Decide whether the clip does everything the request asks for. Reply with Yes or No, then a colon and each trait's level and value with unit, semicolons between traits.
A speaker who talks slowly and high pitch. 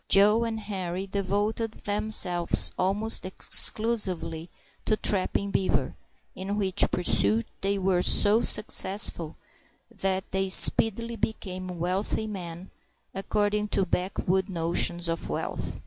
Yes: slow, 110 wpm; high, 195 Hz